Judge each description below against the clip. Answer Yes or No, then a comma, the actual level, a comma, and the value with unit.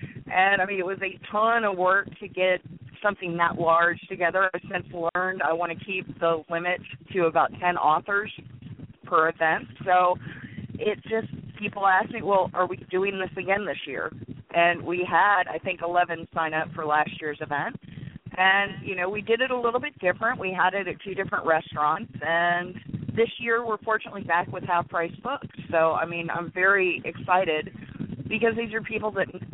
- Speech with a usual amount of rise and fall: Yes, average, 3.1 semitones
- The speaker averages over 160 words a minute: Yes, average, 190 wpm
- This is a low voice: No, medium, 180 Hz